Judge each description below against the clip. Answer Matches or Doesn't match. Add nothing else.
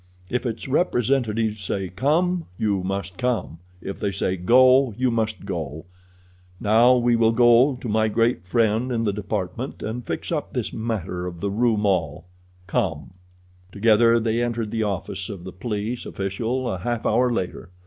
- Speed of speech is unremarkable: Matches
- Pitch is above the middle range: Doesn't match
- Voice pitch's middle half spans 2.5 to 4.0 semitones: Matches